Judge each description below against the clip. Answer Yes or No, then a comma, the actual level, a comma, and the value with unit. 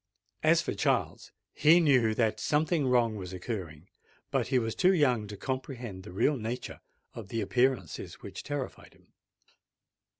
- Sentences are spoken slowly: No, average, 155 wpm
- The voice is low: Yes, low, 120 Hz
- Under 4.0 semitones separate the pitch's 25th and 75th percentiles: No, average, 4.5 semitones